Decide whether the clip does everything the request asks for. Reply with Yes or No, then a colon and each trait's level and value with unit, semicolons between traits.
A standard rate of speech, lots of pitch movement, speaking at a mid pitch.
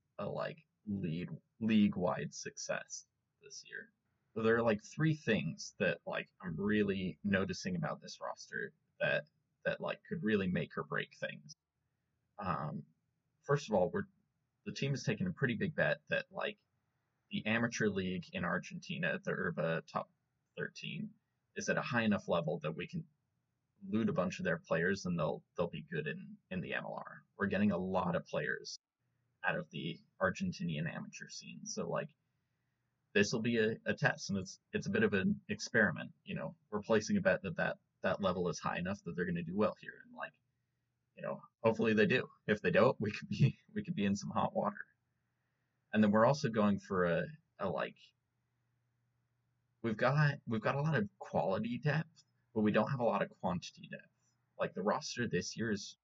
Yes: average, 190 wpm; wide, 8.2 semitones; medium, 155 Hz